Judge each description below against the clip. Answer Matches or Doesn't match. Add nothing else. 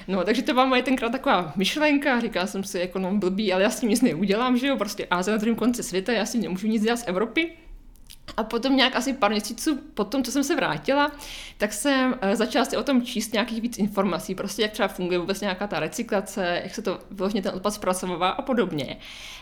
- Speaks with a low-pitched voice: Doesn't match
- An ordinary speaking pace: Doesn't match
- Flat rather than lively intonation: Doesn't match